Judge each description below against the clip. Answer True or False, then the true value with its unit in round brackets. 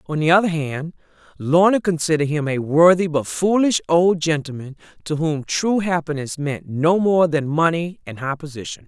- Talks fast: False (170 wpm)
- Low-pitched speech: False (160 Hz)